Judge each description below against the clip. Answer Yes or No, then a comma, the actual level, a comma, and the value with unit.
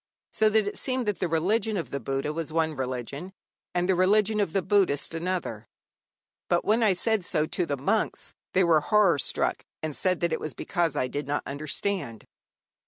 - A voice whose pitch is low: No, medium, 175 Hz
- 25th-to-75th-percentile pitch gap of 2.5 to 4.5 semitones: No, average, 5.3 semitones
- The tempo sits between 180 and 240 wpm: Yes, average, 195 wpm